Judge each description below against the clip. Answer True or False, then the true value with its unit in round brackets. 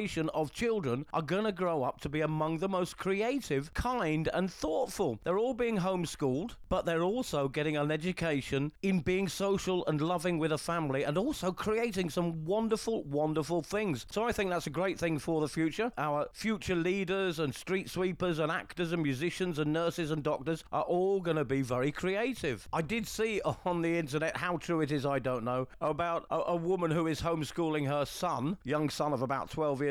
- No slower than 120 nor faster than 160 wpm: False (200 wpm)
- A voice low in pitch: False (165 Hz)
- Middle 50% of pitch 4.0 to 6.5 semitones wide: False (3.6 semitones)